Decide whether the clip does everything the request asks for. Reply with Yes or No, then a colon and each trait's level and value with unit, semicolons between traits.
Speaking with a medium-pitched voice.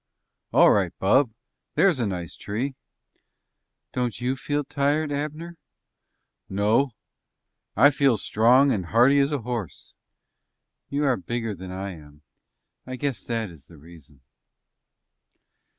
No: low, 120 Hz